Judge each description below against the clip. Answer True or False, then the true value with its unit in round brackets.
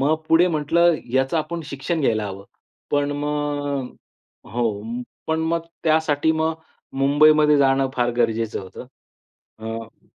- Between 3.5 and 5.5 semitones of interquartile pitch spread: True (4.2 semitones)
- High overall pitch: False (145 Hz)